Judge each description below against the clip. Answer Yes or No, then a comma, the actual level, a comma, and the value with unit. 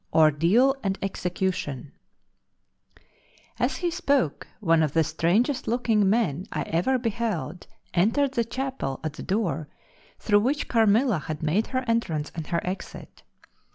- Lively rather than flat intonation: Yes, wide, 6.7 semitones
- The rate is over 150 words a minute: No, slow, 135 wpm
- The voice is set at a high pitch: Yes, high, 195 Hz